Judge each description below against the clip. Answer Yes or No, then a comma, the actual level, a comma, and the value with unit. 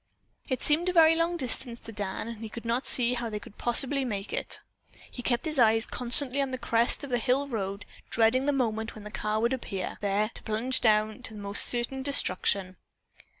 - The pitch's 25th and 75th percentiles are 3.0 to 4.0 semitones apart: Yes, average, 3.6 semitones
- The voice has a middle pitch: No, high, 235 Hz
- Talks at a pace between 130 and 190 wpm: No, fast, 205 wpm